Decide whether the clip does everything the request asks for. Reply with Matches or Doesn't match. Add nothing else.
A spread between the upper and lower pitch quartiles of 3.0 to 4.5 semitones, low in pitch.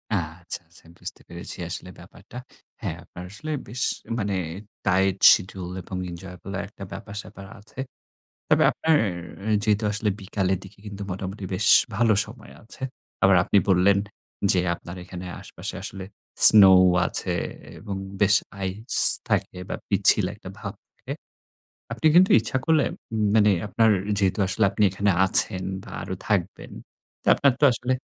Doesn't match